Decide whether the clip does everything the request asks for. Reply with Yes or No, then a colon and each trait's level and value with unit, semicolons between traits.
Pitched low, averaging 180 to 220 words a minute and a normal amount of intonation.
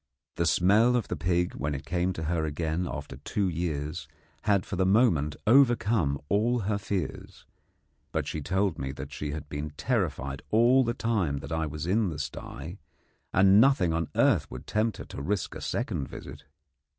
No: very low, 90 Hz; average, 185 wpm; wide, 5.7 semitones